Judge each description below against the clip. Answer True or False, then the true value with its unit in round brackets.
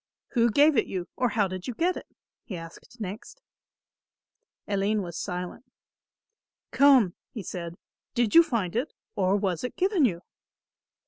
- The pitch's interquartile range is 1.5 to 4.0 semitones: False (5.5 semitones)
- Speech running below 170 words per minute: True (150 wpm)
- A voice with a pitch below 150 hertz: False (210 Hz)